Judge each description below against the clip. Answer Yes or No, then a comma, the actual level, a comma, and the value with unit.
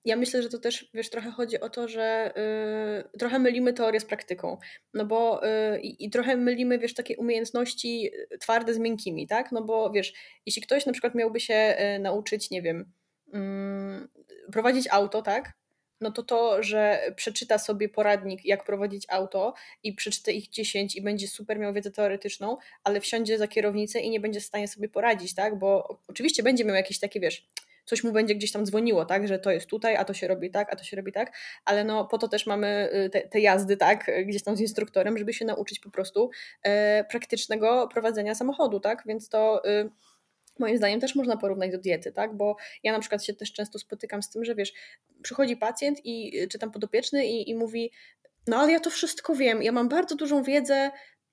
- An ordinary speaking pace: No, fast, 200 wpm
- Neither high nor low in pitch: No, high, 215 Hz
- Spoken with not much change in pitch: Yes, narrow, 2.3 semitones